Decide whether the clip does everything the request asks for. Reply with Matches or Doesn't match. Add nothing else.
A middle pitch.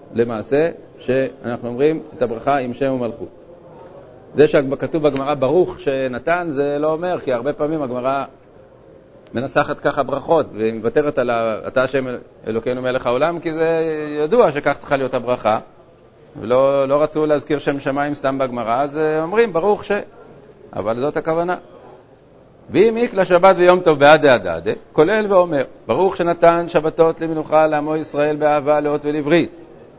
Matches